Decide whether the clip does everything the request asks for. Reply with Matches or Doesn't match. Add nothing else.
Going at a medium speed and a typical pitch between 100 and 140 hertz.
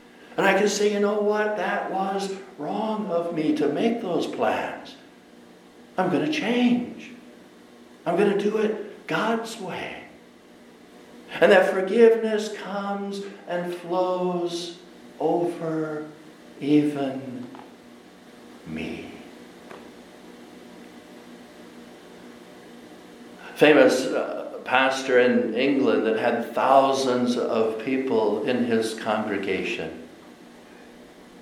Doesn't match